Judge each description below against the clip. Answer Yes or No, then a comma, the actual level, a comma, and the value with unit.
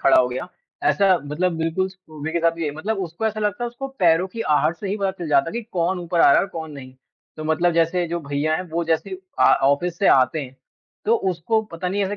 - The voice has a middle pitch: Yes, medium, 170 Hz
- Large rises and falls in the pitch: No, average, 3.4 semitones